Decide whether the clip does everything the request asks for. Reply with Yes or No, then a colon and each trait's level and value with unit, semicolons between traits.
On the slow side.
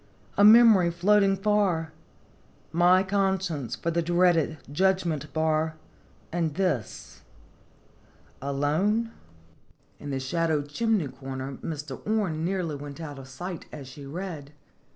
Yes: slow, 115 wpm